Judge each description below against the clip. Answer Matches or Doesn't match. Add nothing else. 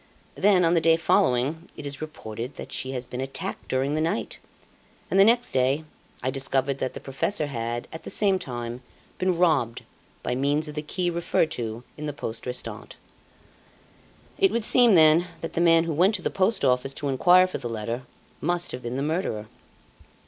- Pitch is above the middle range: Doesn't match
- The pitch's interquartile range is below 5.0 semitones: Doesn't match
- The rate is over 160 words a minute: Matches